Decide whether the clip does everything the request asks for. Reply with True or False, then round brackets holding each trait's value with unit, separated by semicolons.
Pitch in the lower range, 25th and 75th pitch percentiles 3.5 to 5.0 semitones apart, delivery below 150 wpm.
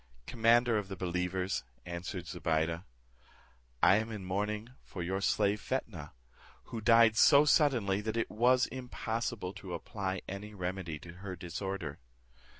True (100 Hz; 3.9 semitones; 140 wpm)